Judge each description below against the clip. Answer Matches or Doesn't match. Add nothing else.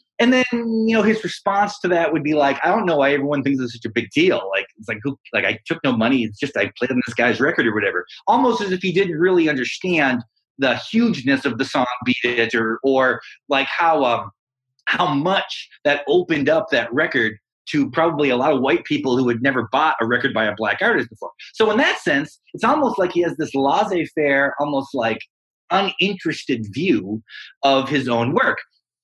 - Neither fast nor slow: Doesn't match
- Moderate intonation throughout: Doesn't match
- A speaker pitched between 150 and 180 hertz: Doesn't match